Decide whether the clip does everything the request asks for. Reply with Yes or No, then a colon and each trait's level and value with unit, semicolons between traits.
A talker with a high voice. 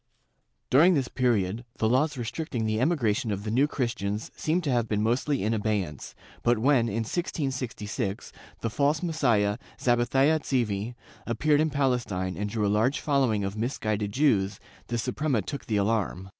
No: low, 115 Hz